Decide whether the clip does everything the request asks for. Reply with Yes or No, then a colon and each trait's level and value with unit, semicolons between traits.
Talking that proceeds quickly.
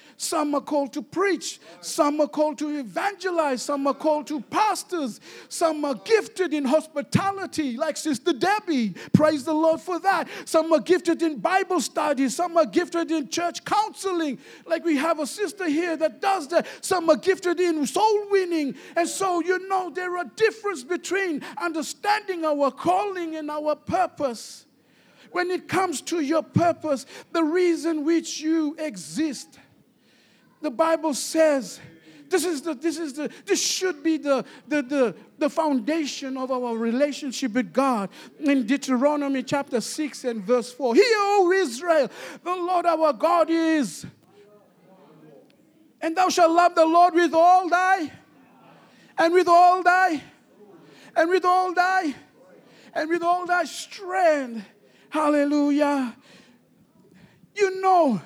No: average, 145 wpm